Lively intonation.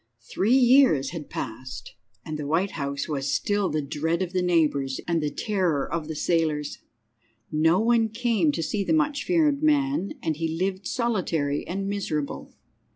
Yes: wide, 6.1 semitones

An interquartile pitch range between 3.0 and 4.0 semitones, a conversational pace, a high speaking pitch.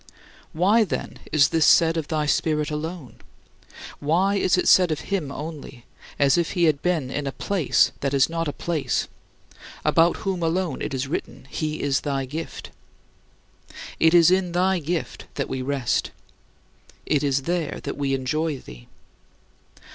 No: average, 3.6 semitones; average, 160 wpm; medium, 155 Hz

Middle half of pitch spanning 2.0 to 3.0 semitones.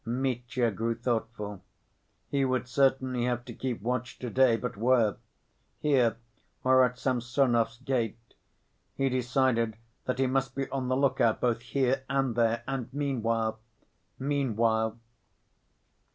Yes: narrow, 2.4 semitones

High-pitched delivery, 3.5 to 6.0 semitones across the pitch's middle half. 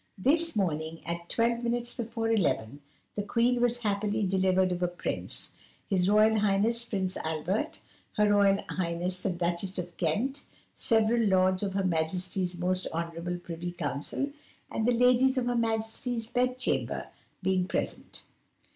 Yes: high, 195 Hz; average, 4.6 semitones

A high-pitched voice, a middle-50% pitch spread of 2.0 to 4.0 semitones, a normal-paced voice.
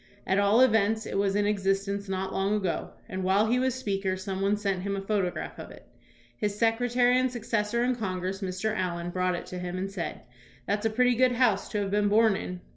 No: high, 200 Hz; average, 2.8 semitones; fast, 230 wpm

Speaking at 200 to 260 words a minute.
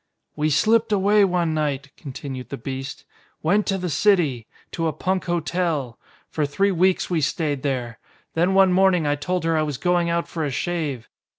No: average, 185 wpm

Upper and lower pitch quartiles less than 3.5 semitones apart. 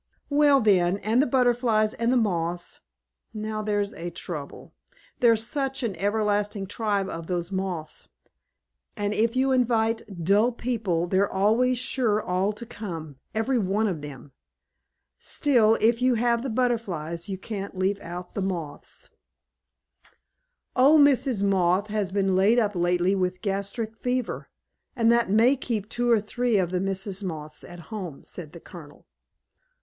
No: average, 4.2 semitones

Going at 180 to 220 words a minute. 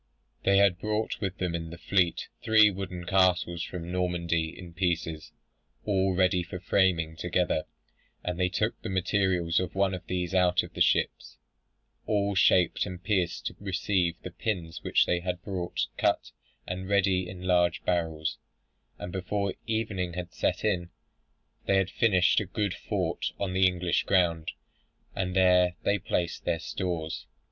No: average, 160 wpm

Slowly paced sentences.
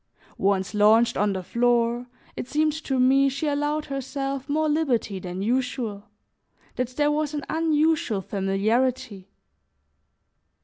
Yes: slow, 125 wpm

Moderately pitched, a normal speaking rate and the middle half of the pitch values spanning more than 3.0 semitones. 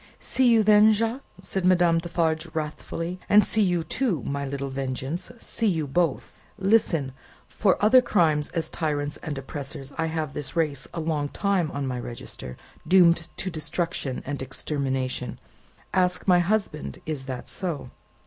Yes: medium, 160 Hz; average, 155 wpm; average, 4.7 semitones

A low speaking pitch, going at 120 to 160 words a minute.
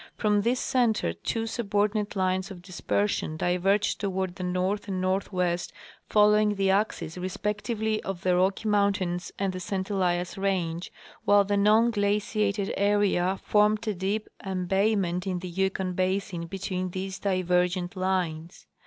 No: high, 195 Hz; average, 145 wpm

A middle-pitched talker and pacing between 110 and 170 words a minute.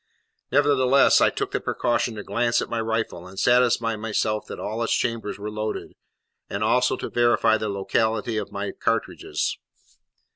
No: low, 110 Hz; average, 160 wpm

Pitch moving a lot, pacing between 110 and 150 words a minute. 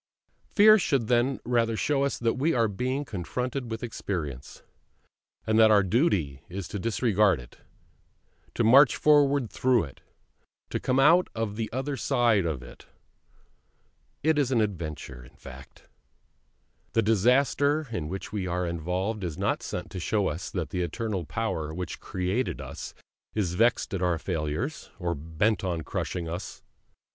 No: wide, 6.1 semitones; average, 160 wpm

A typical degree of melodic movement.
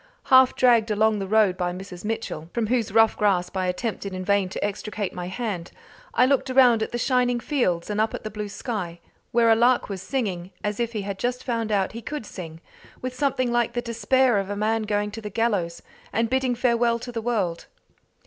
Yes: average, 3.4 semitones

